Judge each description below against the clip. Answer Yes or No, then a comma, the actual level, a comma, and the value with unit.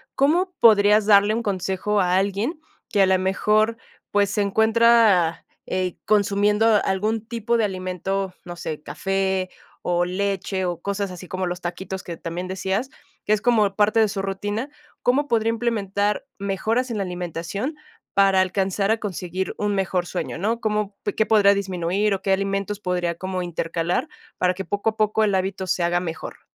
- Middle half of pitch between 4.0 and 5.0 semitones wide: No, narrow, 2.5 semitones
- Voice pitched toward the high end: Yes, high, 195 Hz